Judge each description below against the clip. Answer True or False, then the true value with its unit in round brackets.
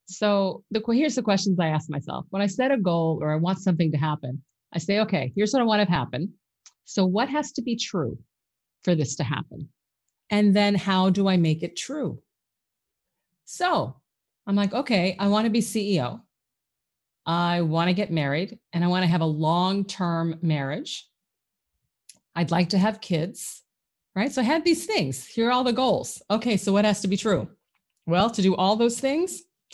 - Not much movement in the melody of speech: False (4.6 semitones)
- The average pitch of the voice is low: False (190 Hz)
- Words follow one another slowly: False (195 wpm)